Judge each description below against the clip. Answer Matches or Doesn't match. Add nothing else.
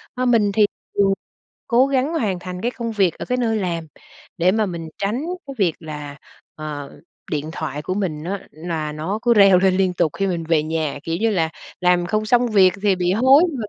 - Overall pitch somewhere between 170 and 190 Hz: Matches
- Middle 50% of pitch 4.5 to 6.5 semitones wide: Matches